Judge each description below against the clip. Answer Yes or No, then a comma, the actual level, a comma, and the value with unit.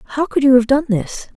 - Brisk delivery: Yes, fast, 255 wpm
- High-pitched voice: Yes, very high, 265 Hz